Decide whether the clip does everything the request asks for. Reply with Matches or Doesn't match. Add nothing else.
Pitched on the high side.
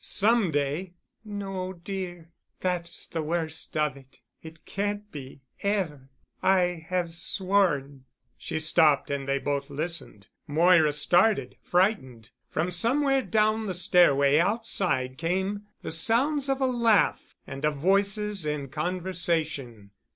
Doesn't match